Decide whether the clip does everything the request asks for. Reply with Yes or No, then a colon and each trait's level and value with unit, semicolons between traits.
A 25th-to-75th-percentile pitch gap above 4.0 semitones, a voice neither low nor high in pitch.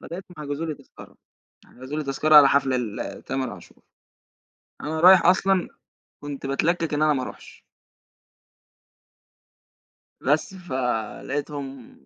No: average, 3.6 semitones; medium, 145 Hz